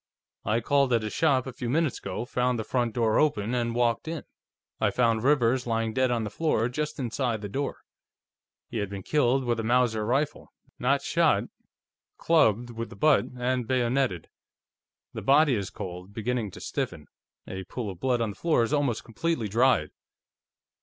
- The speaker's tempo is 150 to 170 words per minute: No, average, 180 wpm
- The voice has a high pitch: No, low, 120 Hz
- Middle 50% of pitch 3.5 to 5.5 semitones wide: No, average, 3.1 semitones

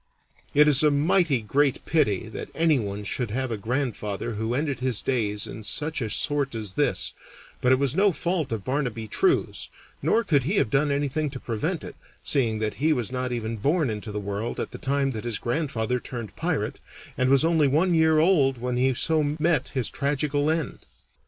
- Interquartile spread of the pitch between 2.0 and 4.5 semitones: No, average, 4.9 semitones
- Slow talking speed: No, average, 195 wpm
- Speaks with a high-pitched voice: No, low, 135 Hz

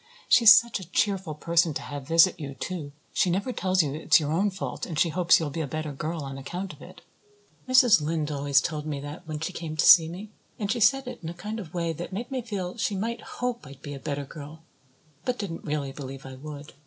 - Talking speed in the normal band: No, fast, 250 wpm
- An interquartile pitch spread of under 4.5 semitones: No, average, 4.9 semitones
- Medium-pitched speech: Yes, medium, 165 Hz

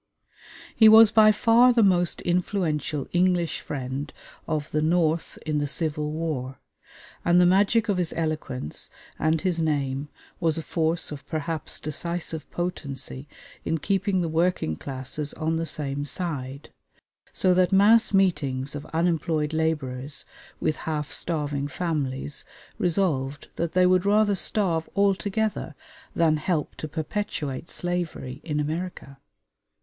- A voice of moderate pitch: Yes, medium, 160 Hz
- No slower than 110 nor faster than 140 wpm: Yes, slow, 135 wpm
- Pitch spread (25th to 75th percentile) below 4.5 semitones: Yes, average, 3.7 semitones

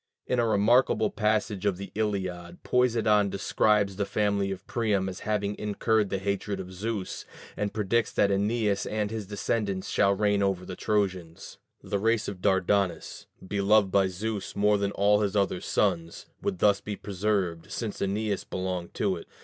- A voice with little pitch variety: Yes, narrow, 1.8 semitones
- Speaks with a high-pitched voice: No, low, 100 Hz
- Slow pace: No, average, 165 wpm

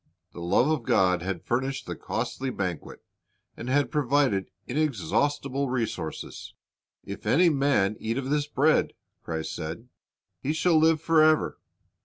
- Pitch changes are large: Yes, wide, 7.2 semitones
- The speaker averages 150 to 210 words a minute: No, slow, 135 wpm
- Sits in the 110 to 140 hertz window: Yes, low, 135 Hz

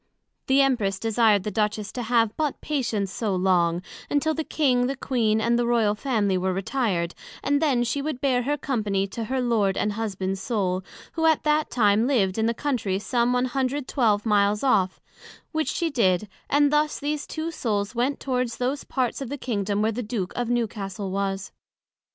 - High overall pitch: Yes, high, 235 Hz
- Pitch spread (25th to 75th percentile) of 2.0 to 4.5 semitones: No, average, 4.9 semitones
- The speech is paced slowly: No, average, 185 wpm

